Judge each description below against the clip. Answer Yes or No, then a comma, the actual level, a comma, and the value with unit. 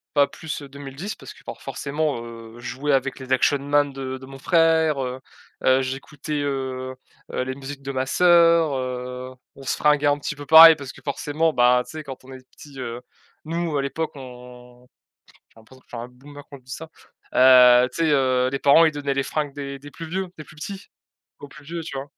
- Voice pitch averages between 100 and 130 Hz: No, medium, 140 Hz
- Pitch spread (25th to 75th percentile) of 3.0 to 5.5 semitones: No, narrow, 2.6 semitones